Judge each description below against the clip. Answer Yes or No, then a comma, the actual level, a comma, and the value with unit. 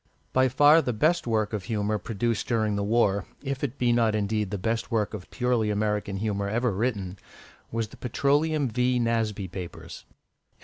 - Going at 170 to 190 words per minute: Yes, average, 175 wpm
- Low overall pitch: Yes, low, 110 Hz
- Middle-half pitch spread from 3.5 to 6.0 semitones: No, average, 3.1 semitones